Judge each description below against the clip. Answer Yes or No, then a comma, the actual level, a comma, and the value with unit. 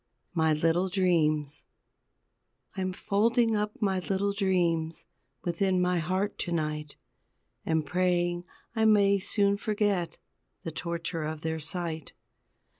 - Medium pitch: Yes, medium, 180 Hz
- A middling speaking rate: No, slow, 115 wpm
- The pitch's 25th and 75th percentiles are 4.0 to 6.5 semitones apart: No, average, 3.6 semitones